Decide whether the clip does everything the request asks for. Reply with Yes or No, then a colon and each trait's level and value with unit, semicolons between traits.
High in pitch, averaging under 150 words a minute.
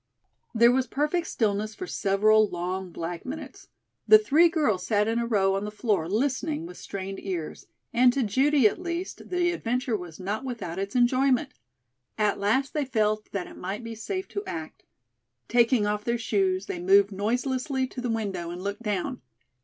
No: high, 230 Hz; average, 180 wpm